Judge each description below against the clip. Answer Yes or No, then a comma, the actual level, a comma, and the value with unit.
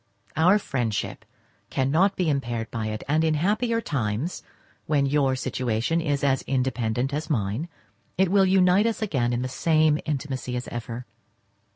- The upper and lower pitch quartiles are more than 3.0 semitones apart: Yes, average, 5.3 semitones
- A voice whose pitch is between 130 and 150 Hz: Yes, medium, 140 Hz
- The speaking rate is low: No, average, 155 wpm